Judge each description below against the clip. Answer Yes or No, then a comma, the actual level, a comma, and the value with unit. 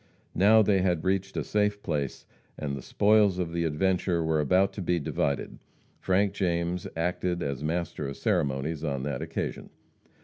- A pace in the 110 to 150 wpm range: No, average, 165 wpm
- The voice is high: No, very low, 85 Hz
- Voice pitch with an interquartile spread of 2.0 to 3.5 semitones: No, average, 4.2 semitones